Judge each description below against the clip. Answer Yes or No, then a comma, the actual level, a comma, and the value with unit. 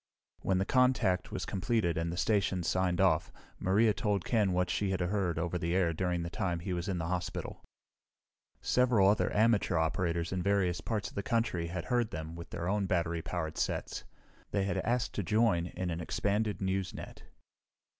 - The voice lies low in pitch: Yes, very low, 95 Hz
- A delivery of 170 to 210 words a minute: Yes, average, 190 wpm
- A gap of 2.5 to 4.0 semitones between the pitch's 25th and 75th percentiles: Yes, average, 3.1 semitones